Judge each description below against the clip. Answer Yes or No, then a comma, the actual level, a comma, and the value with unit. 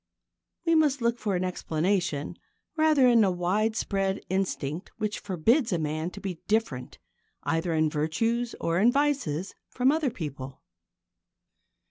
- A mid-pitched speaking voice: No, high, 195 Hz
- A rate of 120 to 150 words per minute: Yes, slow, 135 wpm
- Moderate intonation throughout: No, wide, 6.5 semitones